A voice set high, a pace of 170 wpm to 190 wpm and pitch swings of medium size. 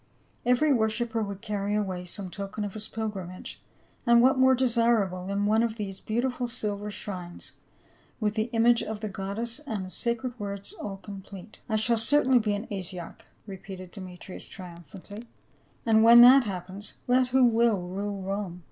Yes: high, 210 Hz; average, 175 wpm; average, 3.3 semitones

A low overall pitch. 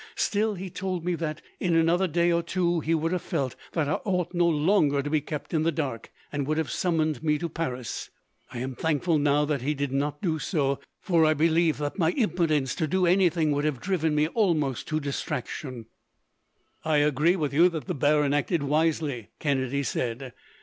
No: medium, 155 Hz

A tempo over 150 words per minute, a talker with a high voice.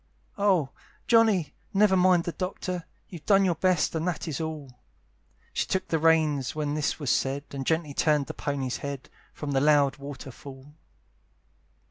No: average, 165 wpm; medium, 155 Hz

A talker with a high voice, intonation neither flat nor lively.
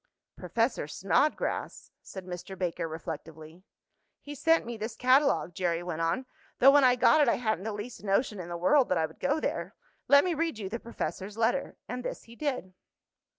No: high, 220 Hz; wide, 6.8 semitones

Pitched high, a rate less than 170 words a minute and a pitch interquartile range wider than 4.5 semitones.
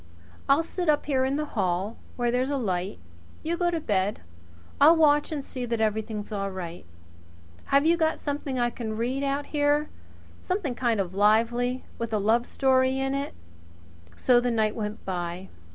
No: high, 245 Hz; average, 180 wpm; average, 5.2 semitones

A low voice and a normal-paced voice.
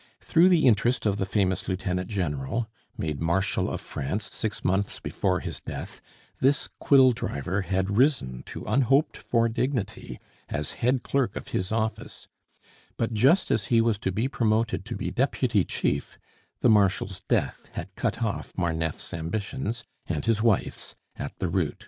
Yes: low, 105 Hz; average, 160 wpm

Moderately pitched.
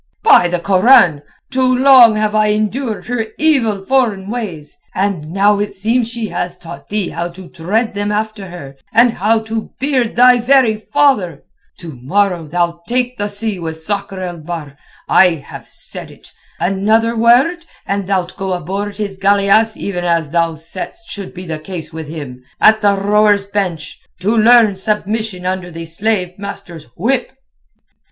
No: high, 200 Hz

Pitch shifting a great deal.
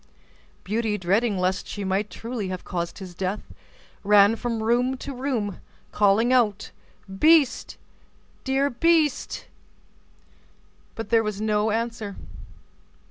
No: average, 3.4 semitones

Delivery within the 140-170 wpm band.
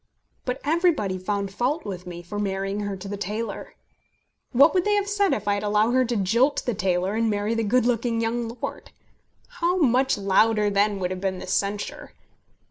No: average, 200 wpm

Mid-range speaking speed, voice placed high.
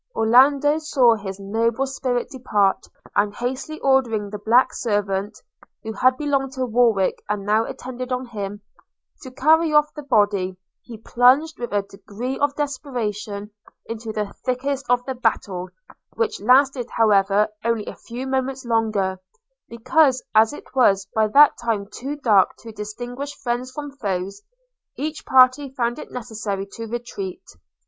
Yes: average, 150 wpm; high, 240 Hz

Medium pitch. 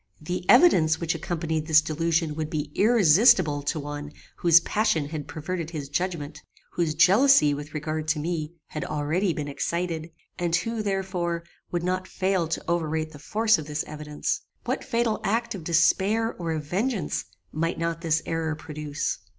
Yes: medium, 165 Hz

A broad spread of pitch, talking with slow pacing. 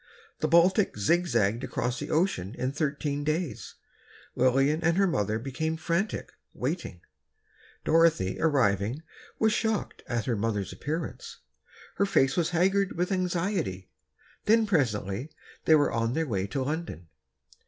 Yes: wide, 6.9 semitones; slow, 130 wpm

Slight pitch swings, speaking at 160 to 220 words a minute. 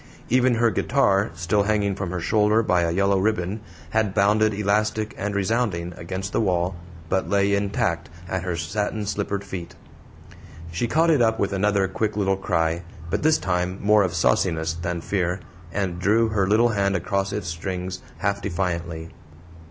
No: average, 3.0 semitones; average, 165 wpm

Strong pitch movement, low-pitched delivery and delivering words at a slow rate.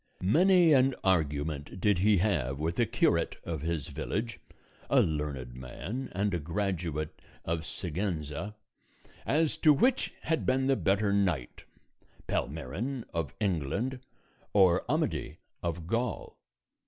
Yes: wide, 6.8 semitones; very low, 90 Hz; slow, 125 wpm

